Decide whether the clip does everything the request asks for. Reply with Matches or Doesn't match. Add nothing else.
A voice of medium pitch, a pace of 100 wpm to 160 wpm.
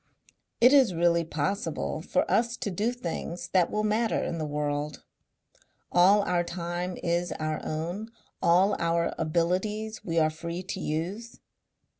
Matches